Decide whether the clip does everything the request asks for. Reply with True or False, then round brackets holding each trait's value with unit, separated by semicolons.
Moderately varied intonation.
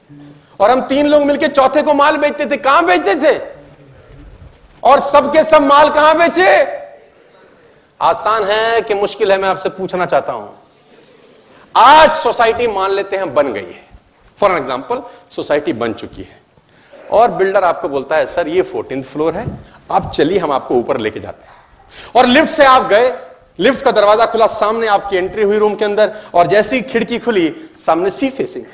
False (6.7 semitones)